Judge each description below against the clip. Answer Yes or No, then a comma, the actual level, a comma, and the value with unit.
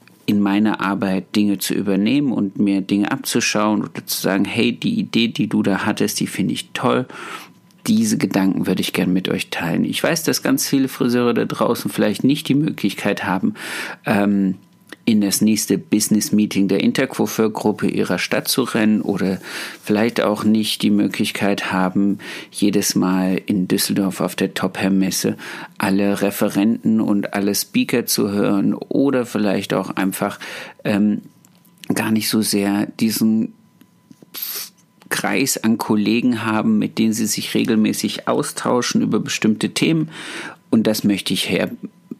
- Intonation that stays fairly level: Yes, narrow, 2.2 semitones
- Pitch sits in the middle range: No, low, 105 Hz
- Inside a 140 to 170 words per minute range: Yes, average, 150 wpm